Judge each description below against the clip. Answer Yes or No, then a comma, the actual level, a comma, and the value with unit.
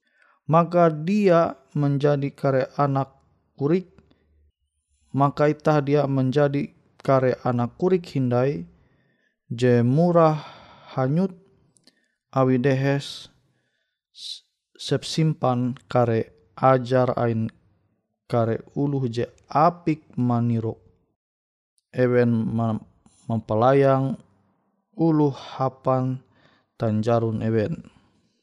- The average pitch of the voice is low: Yes, low, 130 Hz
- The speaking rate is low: Yes, slow, 70 wpm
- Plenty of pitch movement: No, average, 4.1 semitones